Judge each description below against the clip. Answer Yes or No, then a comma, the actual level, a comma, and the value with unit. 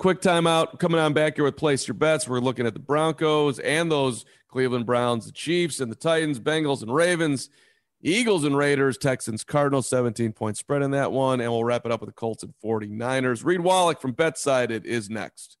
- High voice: No, medium, 140 Hz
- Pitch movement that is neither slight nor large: Yes, average, 4.5 semitones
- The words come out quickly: Yes, fast, 210 wpm